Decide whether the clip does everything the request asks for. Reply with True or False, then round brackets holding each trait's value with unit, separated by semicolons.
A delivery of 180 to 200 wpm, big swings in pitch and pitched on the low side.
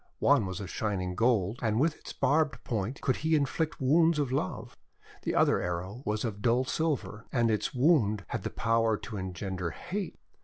True (185 wpm; 5.9 semitones; 115 Hz)